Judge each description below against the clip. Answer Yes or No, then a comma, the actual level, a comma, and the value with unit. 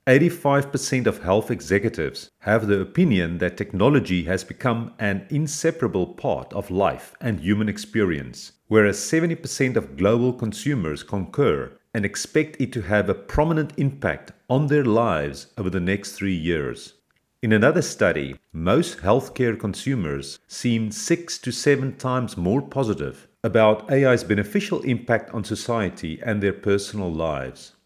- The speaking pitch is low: Yes, low, 115 Hz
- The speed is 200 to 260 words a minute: No, average, 140 wpm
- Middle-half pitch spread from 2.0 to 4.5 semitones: No, average, 5.3 semitones